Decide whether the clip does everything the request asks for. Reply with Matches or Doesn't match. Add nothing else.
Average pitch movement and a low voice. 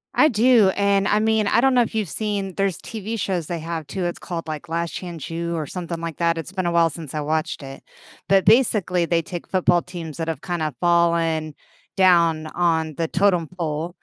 Doesn't match